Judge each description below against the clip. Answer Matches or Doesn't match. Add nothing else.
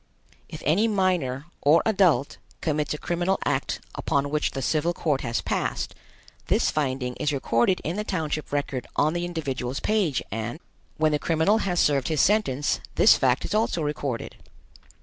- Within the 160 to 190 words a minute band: Matches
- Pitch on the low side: Doesn't match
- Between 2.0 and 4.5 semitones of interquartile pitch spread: Matches